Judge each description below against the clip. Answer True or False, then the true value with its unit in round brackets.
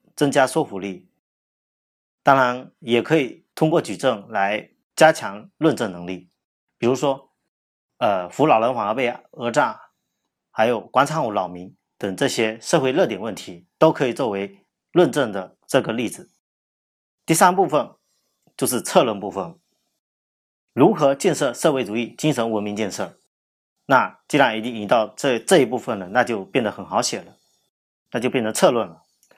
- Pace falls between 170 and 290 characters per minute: True (230 characters per minute)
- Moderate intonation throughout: False (6.4 semitones)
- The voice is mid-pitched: False (115 Hz)